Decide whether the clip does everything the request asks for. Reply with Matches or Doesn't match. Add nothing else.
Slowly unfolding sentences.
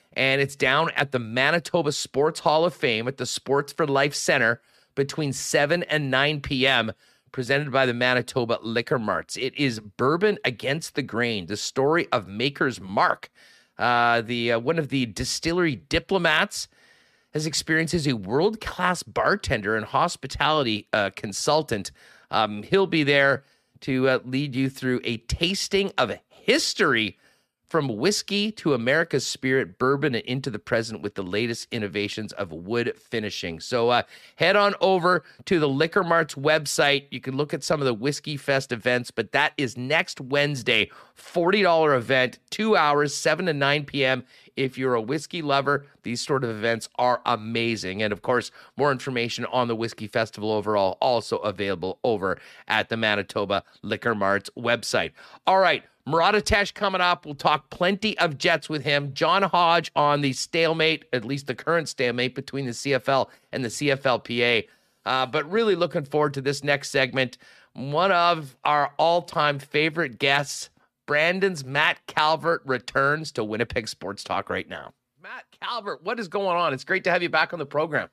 Doesn't match